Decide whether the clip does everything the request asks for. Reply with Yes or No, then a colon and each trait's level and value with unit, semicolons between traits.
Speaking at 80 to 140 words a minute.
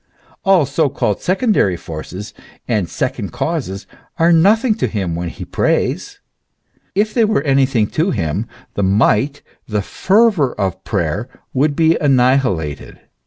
Yes: slow, 135 wpm